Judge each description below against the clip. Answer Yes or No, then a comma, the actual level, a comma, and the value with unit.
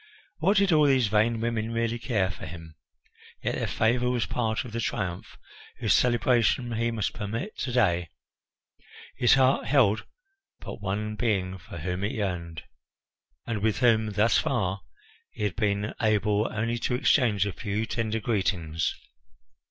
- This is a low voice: Yes, low, 110 Hz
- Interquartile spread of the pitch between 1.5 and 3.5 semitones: Yes, average, 3.1 semitones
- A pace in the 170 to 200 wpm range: No, average, 155 wpm